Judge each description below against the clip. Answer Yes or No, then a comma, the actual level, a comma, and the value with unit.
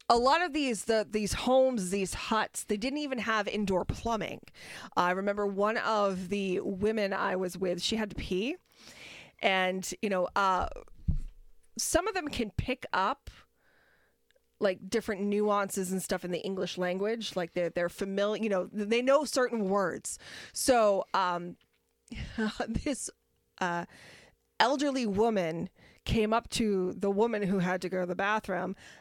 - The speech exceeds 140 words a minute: Yes, average, 155 wpm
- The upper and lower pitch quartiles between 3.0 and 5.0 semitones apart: Yes, average, 3.5 semitones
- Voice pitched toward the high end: Yes, high, 205 Hz